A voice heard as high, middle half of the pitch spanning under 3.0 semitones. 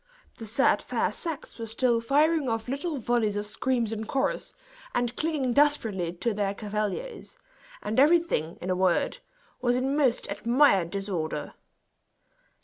No: high, 235 Hz; average, 5.0 semitones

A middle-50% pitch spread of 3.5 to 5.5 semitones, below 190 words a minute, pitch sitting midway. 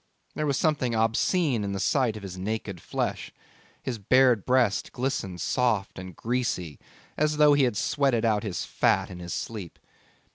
No: average, 5.0 semitones; average, 170 wpm; low, 115 Hz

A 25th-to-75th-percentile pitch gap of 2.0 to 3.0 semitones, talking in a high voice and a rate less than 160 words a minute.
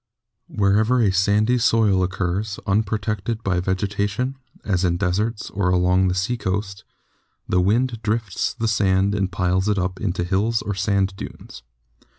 No: narrow, 2.5 semitones; low, 100 Hz; average, 150 wpm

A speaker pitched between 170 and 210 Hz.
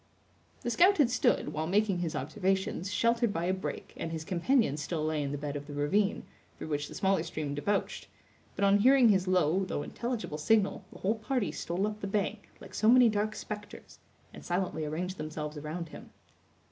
Yes: high, 190 Hz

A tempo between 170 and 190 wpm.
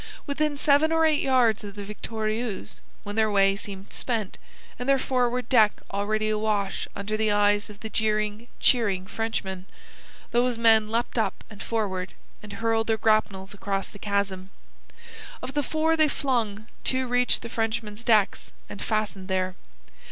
No: average, 160 wpm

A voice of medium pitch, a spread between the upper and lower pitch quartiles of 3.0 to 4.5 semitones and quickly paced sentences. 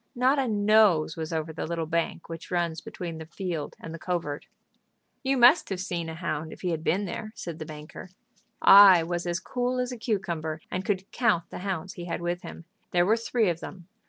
Yes: medium, 175 Hz; average, 4.0 semitones; fast, 215 wpm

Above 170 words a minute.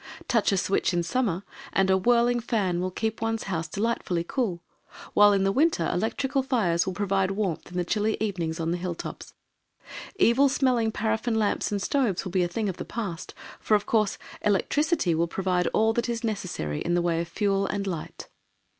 Yes: average, 200 wpm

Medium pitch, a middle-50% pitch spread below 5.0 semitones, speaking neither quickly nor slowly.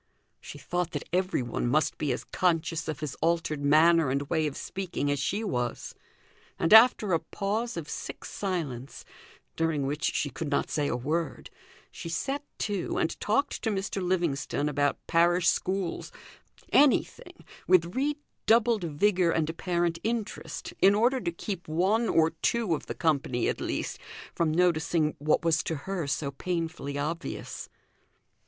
Yes: medium, 165 Hz; average, 4.2 semitones; average, 155 wpm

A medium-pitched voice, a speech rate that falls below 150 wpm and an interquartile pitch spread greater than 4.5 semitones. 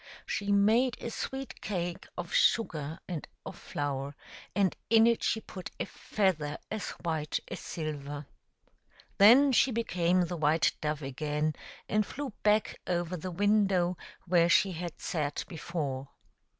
Yes: medium, 175 Hz; average, 140 wpm; average, 5.3 semitones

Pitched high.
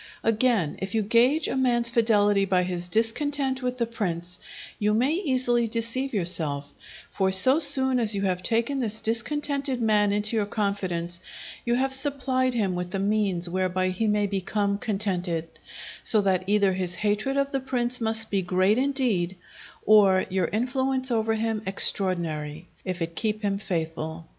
Yes: high, 210 Hz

